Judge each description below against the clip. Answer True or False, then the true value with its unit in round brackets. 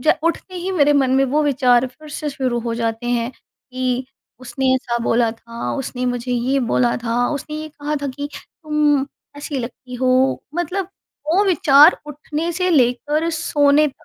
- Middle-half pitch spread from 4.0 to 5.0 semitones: False (3.5 semitones)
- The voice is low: False (270 Hz)